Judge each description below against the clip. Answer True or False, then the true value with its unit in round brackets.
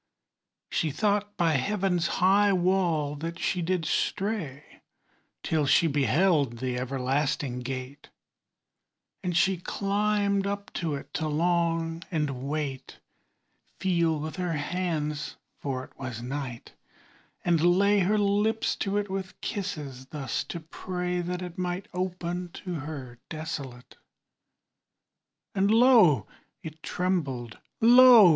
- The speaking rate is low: True (120 wpm)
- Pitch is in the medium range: True (170 Hz)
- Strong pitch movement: False (4.8 semitones)